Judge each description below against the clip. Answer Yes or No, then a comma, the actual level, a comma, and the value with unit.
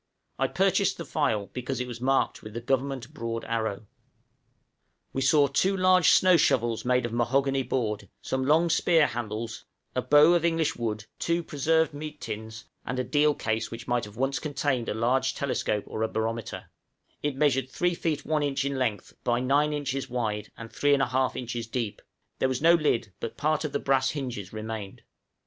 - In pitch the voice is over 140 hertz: No, low, 130 Hz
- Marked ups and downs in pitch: No, average, 4.2 semitones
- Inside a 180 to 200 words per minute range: Yes, average, 185 wpm